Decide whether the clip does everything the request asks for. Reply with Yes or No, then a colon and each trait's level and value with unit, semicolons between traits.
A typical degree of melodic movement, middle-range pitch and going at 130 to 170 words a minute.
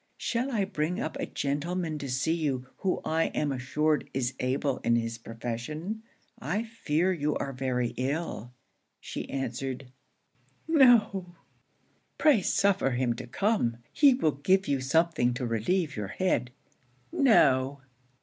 No: wide, 6.5 semitones; medium, 150 Hz; average, 140 wpm